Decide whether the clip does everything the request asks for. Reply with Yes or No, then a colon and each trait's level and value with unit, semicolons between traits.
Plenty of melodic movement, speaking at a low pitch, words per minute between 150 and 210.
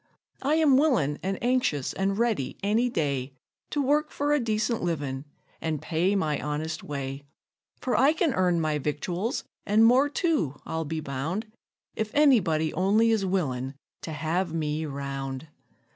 No: wide, 7.8 semitones; medium, 180 Hz; average, 160 wpm